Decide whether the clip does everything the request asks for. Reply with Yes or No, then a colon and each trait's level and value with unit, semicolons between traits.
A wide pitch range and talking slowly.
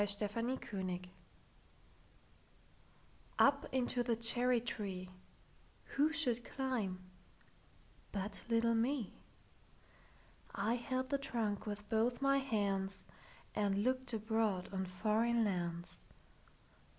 No: average, 3.8 semitones; slow, 85 wpm